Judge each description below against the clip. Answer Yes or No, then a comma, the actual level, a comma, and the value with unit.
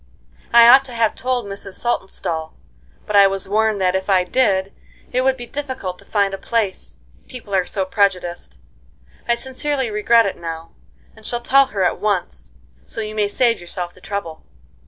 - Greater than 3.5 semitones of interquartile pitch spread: Yes, average, 4.1 semitones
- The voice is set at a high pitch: Yes, high, 205 Hz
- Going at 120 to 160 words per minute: No, average, 180 wpm